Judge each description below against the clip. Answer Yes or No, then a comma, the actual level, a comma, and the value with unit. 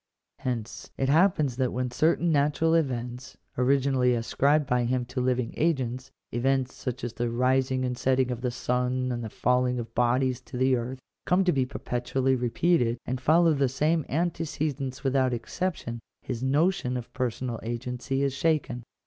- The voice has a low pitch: Yes, low, 130 Hz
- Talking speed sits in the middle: Yes, average, 170 wpm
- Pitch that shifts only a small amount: Yes, narrow, 2.2 semitones